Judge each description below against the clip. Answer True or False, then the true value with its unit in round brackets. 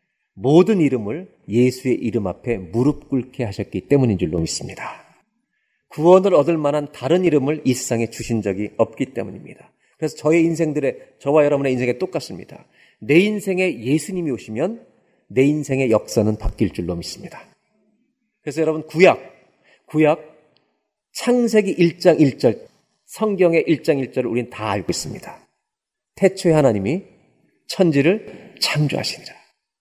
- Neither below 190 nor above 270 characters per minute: False (300 characters per minute)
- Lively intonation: True (6.1 semitones)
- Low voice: False (145 Hz)